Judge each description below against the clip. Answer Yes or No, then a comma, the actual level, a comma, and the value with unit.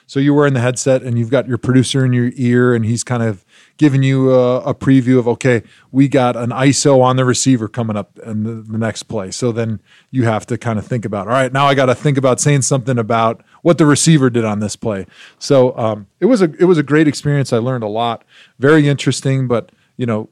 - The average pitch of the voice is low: Yes, low, 125 Hz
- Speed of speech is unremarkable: No, fast, 250 wpm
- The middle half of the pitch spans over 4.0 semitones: No, average, 3.1 semitones